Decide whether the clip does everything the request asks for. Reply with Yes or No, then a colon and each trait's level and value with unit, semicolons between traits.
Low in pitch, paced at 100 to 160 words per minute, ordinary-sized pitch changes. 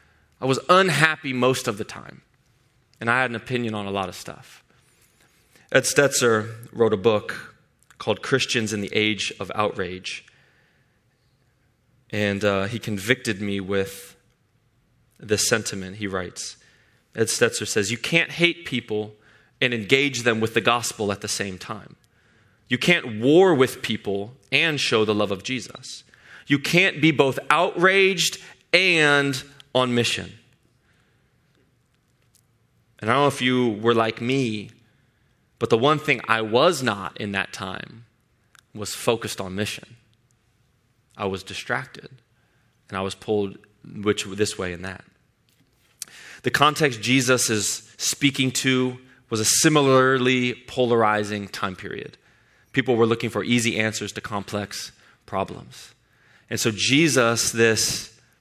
Yes: low, 120 Hz; average, 140 wpm; average, 3.5 semitones